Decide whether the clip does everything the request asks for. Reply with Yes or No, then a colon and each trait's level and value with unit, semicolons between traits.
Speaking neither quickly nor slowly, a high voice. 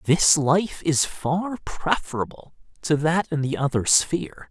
No: average, 145 wpm; medium, 155 Hz